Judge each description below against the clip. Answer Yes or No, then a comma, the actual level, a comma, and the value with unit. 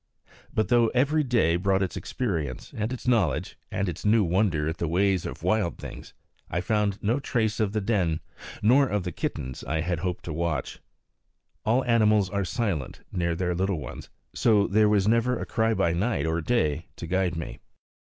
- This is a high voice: No, very low, 95 Hz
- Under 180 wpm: No, average, 190 wpm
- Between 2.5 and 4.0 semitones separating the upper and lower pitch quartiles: No, average, 4.6 semitones